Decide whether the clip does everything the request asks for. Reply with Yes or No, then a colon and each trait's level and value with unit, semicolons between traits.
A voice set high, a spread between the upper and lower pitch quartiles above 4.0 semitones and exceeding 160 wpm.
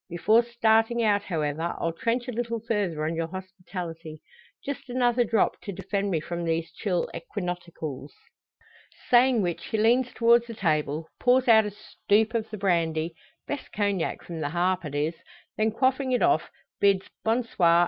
Yes: high, 200 Hz; wide, 5.6 semitones; average, 170 wpm